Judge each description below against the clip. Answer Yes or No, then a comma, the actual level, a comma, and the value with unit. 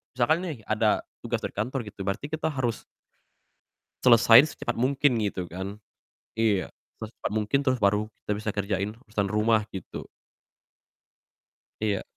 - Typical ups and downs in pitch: Yes, average, 3.0 semitones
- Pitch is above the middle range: No, low, 110 Hz